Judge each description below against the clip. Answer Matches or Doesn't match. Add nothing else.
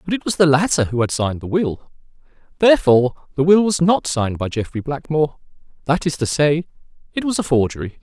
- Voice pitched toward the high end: Doesn't match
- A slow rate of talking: Doesn't match